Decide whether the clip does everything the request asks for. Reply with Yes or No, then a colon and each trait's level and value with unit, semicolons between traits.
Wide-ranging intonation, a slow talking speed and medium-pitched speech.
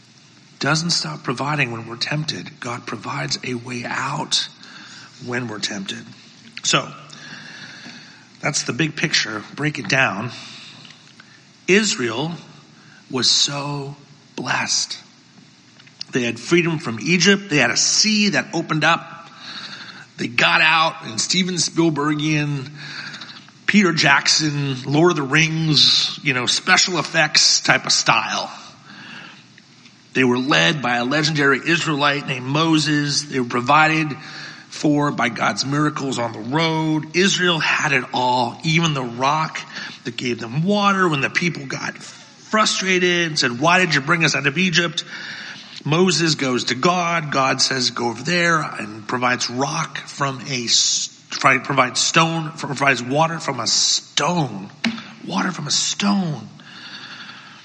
No: average, 4.4 semitones; slow, 130 wpm; medium, 150 Hz